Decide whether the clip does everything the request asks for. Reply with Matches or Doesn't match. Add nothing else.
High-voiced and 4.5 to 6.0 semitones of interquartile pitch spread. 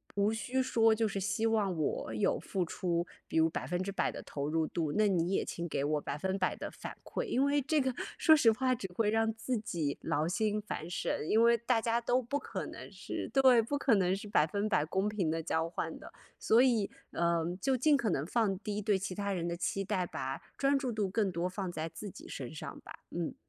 Matches